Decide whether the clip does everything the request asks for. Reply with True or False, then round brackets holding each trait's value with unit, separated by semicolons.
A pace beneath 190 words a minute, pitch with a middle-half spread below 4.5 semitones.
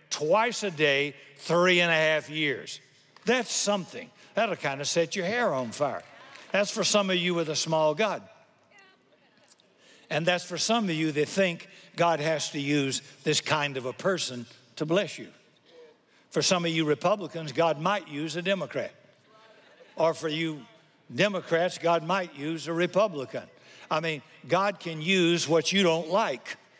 True (170 wpm; 3.8 semitones)